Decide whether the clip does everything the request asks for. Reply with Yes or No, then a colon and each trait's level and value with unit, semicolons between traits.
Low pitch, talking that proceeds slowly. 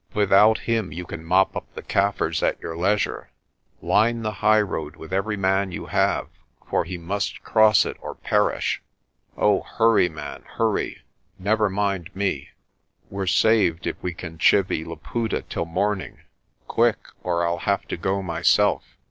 No: very low, 95 Hz; average, 155 wpm